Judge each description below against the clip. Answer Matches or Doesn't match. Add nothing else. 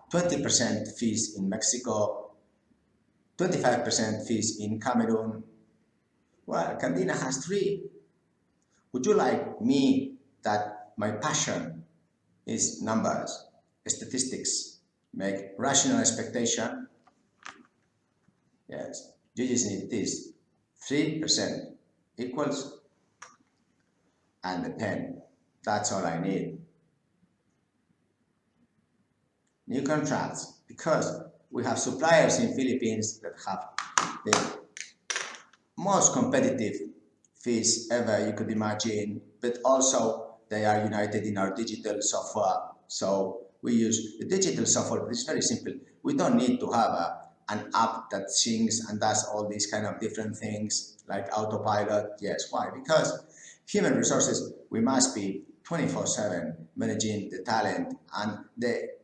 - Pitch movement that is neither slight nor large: Matches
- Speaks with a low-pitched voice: Matches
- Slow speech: Matches